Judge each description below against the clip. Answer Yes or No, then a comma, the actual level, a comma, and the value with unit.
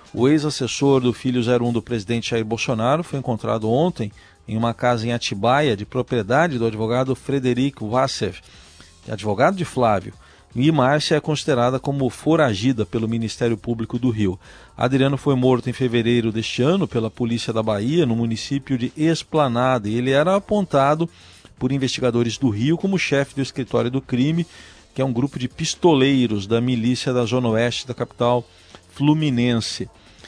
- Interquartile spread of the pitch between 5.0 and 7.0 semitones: No, average, 3.1 semitones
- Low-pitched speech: Yes, low, 125 Hz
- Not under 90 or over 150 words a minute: No, average, 160 wpm